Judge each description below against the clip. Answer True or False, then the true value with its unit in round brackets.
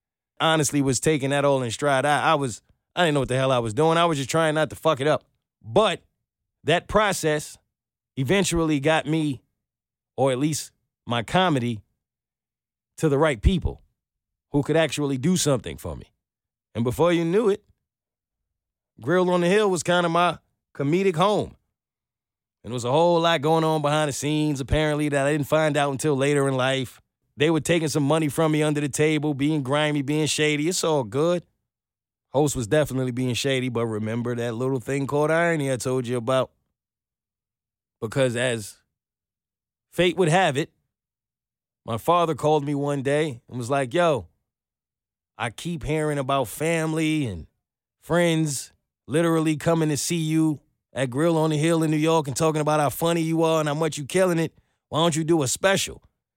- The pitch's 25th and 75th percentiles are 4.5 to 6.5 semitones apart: False (3.5 semitones)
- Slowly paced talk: False (185 wpm)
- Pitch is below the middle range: False (150 Hz)